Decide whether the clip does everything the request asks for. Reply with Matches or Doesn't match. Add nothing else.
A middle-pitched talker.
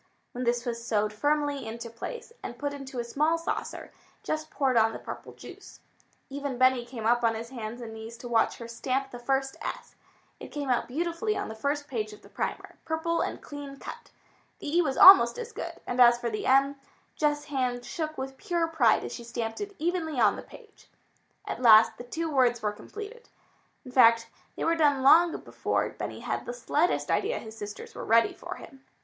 Doesn't match